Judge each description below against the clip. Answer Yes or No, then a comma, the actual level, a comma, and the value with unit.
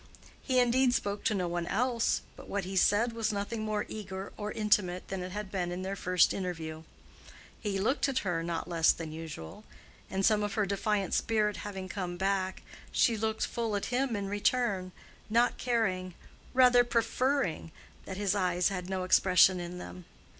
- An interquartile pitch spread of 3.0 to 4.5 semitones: Yes, average, 3.4 semitones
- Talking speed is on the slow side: No, average, 175 wpm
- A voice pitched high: Yes, high, 195 Hz